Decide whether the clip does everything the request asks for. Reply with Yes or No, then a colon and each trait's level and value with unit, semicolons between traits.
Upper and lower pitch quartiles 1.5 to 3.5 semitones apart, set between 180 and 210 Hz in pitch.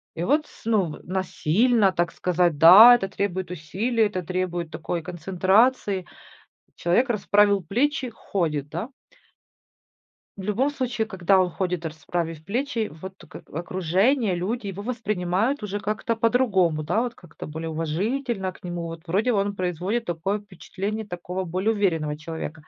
No: average, 4.2 semitones; high, 190 Hz